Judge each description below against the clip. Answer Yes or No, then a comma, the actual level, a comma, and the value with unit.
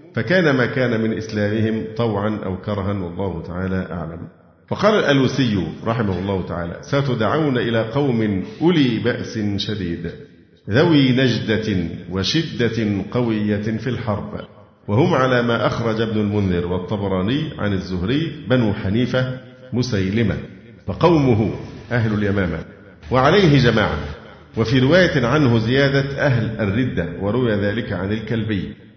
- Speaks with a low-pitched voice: Yes, low, 110 Hz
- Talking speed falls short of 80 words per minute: No, average, 115 wpm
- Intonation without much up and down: No, average, 4.4 semitones